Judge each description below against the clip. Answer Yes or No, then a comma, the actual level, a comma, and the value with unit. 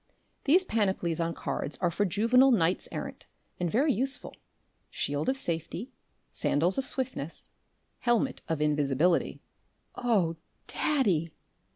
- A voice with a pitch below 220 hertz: Yes, medium, 185 Hz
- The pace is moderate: No, slow, 115 wpm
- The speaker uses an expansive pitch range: Yes, wide, 7.5 semitones